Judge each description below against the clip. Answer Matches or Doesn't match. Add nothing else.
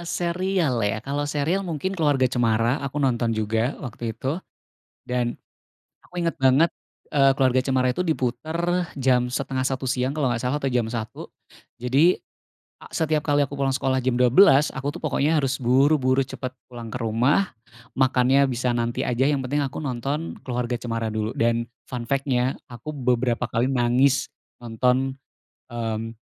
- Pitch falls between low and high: Doesn't match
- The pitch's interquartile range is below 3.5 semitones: Matches